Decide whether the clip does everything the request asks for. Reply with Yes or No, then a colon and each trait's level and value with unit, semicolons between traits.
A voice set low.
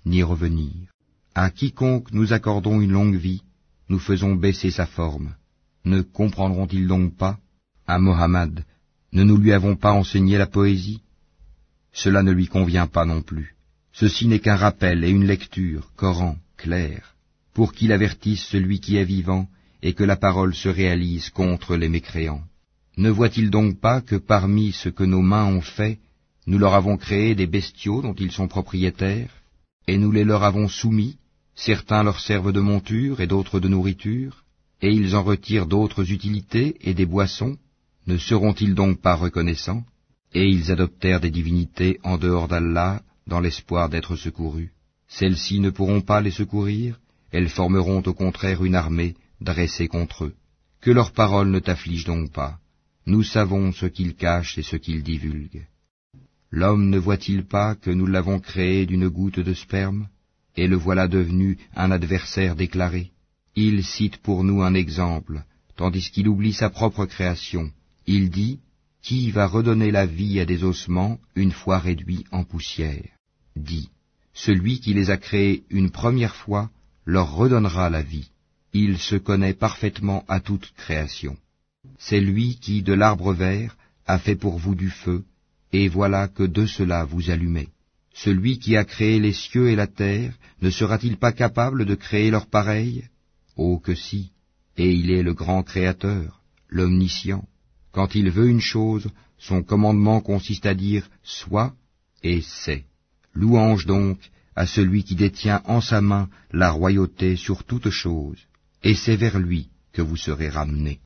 Yes: very low, 95 Hz